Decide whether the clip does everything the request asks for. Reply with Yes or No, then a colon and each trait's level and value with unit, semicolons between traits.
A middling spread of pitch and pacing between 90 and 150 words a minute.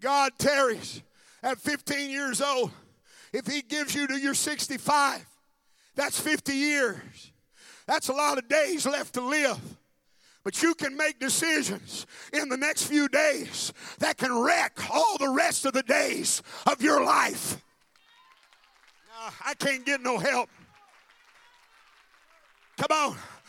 No: narrow, 2.0 semitones; average, 140 wpm